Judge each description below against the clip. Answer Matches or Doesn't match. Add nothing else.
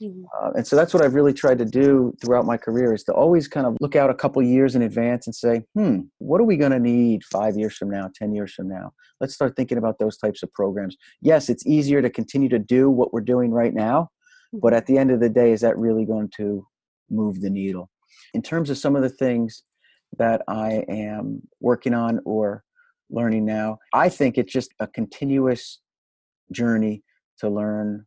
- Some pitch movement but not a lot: Matches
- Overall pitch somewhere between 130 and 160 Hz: Doesn't match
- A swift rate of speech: Matches